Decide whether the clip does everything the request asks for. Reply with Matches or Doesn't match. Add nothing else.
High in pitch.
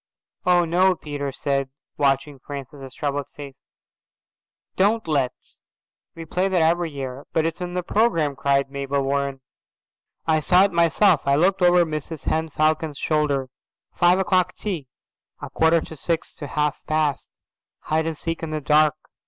Doesn't match